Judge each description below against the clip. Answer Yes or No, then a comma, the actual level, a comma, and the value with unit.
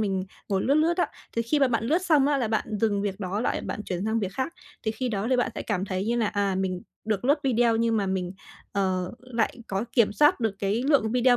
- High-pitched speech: Yes, high, 220 Hz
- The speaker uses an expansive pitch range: No, average, 4.1 semitones